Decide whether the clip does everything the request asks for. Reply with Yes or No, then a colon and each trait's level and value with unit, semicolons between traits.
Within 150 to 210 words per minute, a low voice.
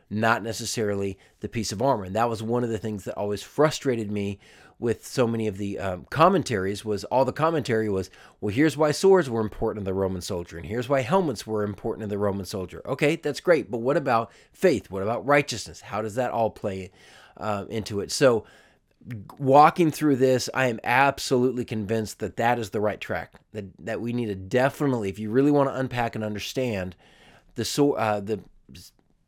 Yes: average, 200 wpm; low, 110 Hz